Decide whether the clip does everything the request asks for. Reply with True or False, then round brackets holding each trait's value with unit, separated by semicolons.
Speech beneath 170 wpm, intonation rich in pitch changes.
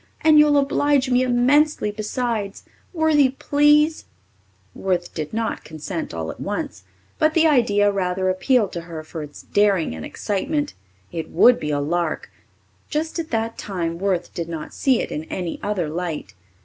True (160 wpm; 8.4 semitones)